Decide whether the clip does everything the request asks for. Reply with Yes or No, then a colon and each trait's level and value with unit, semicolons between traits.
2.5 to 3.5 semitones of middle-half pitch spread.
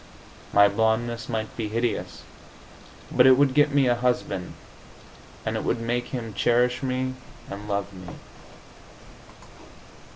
Yes: average, 2.9 semitones